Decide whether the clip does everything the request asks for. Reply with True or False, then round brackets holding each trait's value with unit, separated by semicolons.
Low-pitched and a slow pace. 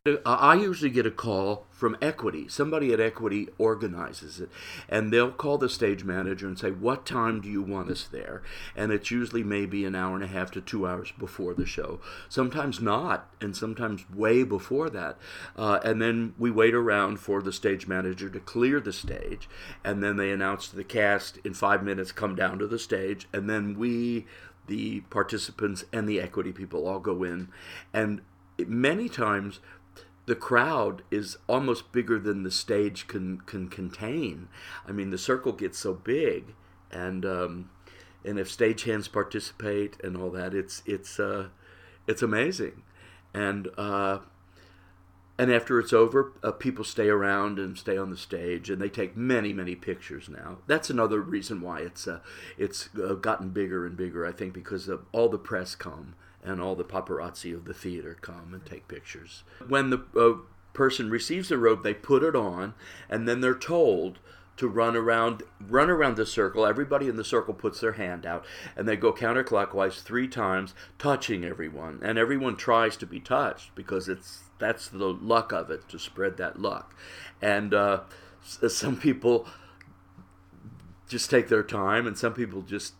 False (100 Hz; 175 wpm)